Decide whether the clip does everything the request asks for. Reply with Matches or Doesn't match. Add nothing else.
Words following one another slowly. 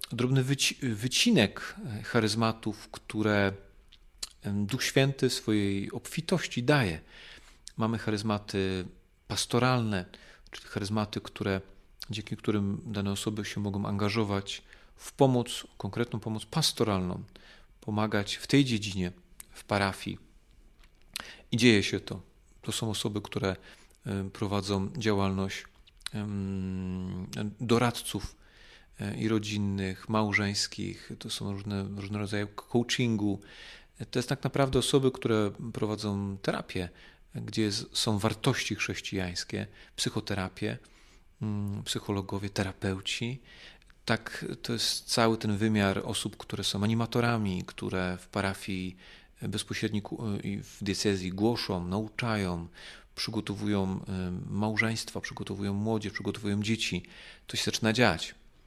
Matches